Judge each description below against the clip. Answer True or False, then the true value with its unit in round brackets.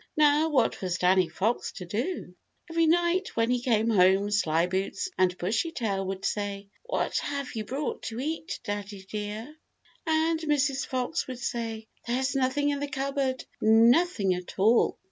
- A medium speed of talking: True (160 wpm)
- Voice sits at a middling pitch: False (235 Hz)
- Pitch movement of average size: False (6.4 semitones)